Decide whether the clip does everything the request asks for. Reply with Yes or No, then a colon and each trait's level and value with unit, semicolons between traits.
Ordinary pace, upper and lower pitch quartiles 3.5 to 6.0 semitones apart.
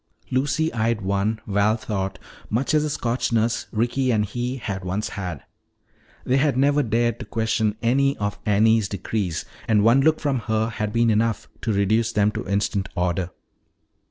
No: average, 165 wpm; average, 3.0 semitones